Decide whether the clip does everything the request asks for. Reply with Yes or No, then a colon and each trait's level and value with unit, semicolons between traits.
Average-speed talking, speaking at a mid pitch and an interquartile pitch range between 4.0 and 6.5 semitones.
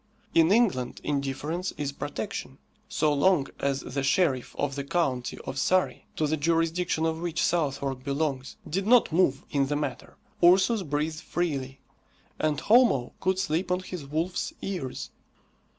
Yes: average, 150 wpm; medium, 155 Hz; average, 4.4 semitones